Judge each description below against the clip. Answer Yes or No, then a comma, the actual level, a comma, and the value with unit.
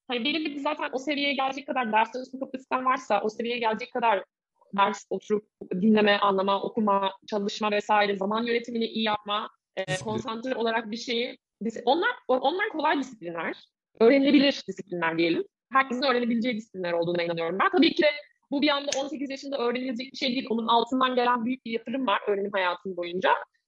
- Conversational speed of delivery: No, fast, 165 wpm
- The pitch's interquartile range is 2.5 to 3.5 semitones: No, average, 4.5 semitones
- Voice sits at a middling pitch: No, high, 240 Hz